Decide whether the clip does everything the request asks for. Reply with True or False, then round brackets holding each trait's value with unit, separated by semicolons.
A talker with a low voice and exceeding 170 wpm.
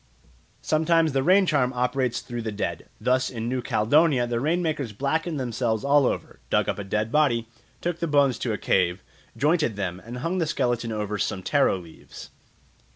True (125 Hz; 185 wpm)